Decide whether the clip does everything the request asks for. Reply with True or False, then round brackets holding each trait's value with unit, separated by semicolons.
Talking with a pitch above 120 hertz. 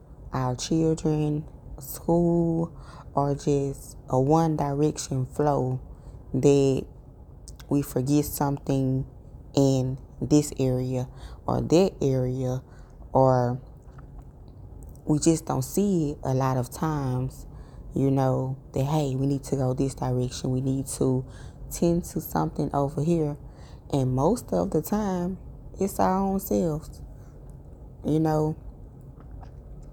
True (140 Hz)